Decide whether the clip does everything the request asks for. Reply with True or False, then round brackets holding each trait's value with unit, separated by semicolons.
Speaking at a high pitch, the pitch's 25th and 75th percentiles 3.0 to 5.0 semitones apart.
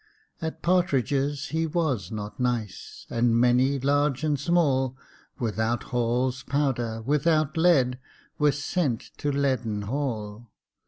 False (135 Hz; 3.7 semitones)